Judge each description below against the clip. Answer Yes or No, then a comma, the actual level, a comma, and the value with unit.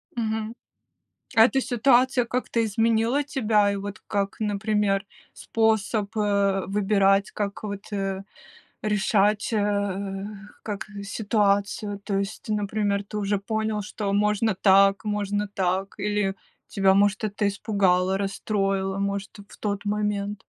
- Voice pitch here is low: No, high, 205 Hz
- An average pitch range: No, narrow, 1.5 semitones